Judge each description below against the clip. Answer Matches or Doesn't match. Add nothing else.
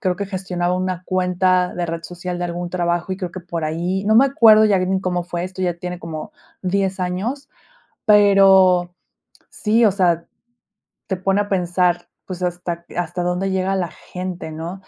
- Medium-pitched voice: Matches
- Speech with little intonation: Matches